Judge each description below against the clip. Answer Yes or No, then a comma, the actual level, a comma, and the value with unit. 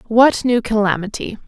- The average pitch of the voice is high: Yes, high, 225 Hz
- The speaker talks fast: No, slow, 120 wpm